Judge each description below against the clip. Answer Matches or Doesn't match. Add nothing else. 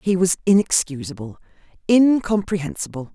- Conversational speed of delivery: Doesn't match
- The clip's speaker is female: Matches